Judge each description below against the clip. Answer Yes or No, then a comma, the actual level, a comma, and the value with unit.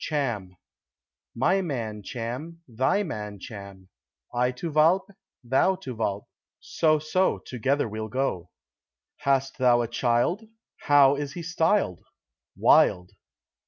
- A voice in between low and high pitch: No, low, 130 Hz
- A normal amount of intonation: No, wide, 6.0 semitones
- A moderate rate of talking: No, slow, 120 wpm